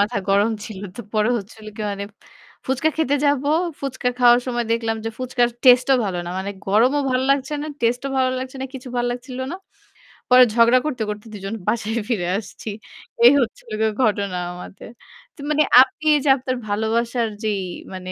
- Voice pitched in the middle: No, high, 240 Hz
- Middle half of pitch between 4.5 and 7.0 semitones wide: No, average, 3.3 semitones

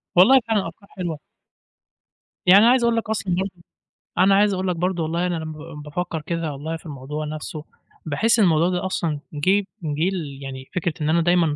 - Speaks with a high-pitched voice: No, medium, 170 Hz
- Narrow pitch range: No, average, 3.6 semitones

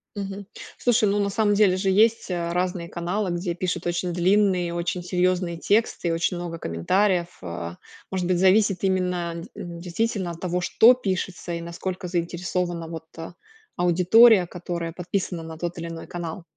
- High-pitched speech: No, medium, 180 Hz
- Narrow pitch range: Yes, narrow, 2.1 semitones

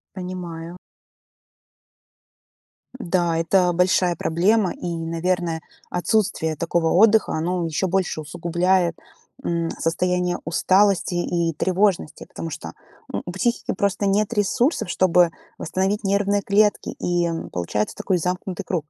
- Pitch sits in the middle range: Yes, medium, 180 Hz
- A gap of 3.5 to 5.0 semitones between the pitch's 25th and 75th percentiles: No, narrow, 2.4 semitones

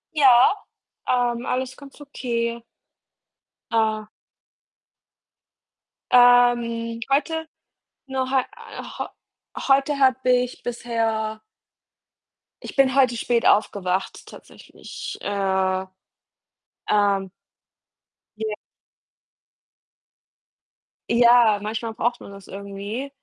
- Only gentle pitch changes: No, average, 3.2 semitones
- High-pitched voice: Yes, high, 235 Hz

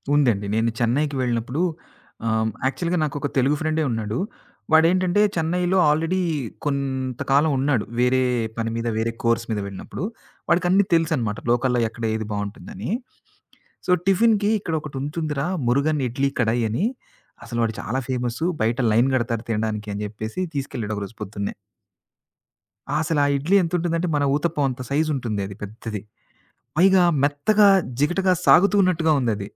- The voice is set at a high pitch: No, low, 135 Hz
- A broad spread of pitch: Yes, wide, 6.2 semitones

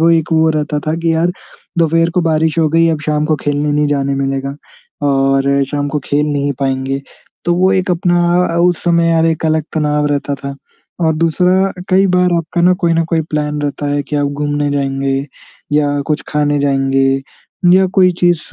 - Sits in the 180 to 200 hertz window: No, medium, 150 Hz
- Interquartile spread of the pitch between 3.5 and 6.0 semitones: No, average, 2.8 semitones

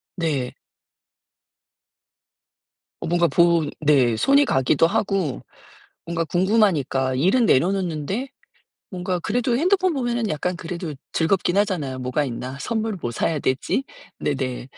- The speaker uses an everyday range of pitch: No, wide, 6.5 semitones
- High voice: No, medium, 170 Hz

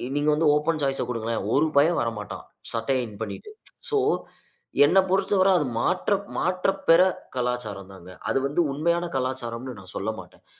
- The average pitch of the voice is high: No, low, 135 Hz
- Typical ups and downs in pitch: No, wide, 6.4 semitones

